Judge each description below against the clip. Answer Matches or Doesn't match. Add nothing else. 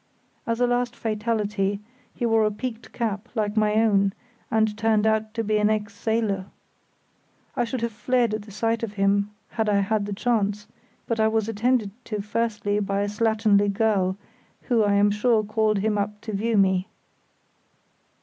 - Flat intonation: Matches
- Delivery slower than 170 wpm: Doesn't match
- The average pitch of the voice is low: Doesn't match